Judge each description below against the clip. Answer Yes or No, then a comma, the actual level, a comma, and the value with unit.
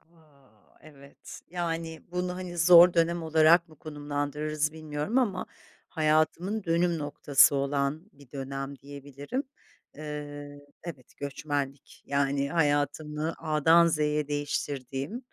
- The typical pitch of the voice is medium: Yes, medium, 150 Hz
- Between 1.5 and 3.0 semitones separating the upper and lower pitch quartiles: Yes, average, 2.7 semitones